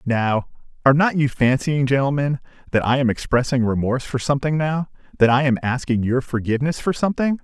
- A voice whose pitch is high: No, low, 135 Hz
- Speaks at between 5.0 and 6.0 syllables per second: Yes, 5.9 syllables/s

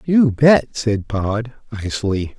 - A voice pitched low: Yes, low, 115 Hz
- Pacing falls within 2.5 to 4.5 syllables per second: Yes, 3.4 syllables/s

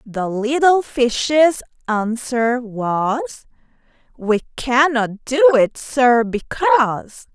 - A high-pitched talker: Yes, very high, 250 Hz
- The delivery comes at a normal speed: No, slow, 90 wpm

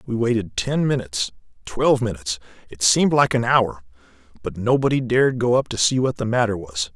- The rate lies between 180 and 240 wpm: Yes, average, 190 wpm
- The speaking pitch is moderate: No, low, 110 Hz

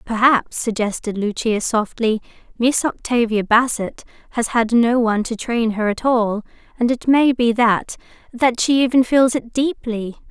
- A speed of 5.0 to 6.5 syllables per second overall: No, 4.4 syllables/s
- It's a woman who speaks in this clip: Yes, female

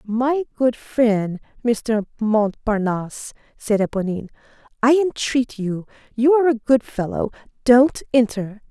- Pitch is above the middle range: Yes, high, 230 Hz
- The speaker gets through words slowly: Yes, slow, 115 wpm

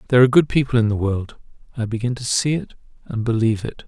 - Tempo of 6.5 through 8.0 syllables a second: Yes, 7.0 syllables/s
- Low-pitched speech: Yes, low, 120 Hz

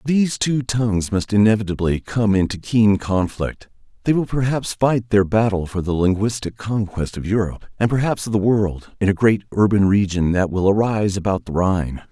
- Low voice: Yes, low, 105 Hz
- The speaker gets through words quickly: No, average, 185 wpm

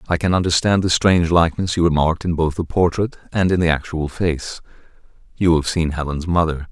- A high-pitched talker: No, very low, 85 Hz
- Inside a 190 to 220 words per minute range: Yes, average, 195 wpm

